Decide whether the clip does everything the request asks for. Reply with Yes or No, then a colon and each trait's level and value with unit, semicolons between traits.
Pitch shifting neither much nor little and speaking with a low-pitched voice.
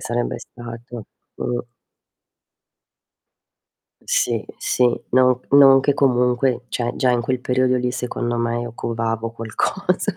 No: narrow, 1.4 semitones; low, 125 Hz